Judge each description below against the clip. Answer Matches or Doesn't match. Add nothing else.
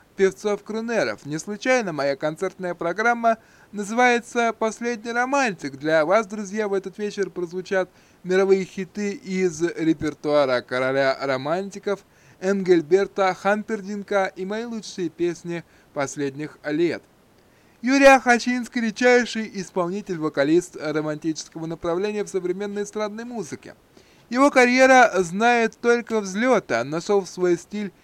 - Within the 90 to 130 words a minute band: Matches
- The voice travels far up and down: Doesn't match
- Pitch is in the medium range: Doesn't match